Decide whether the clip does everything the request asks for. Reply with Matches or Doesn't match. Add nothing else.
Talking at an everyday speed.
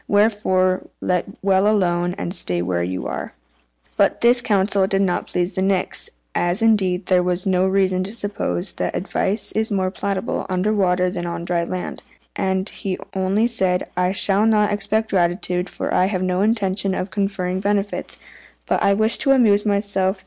Matches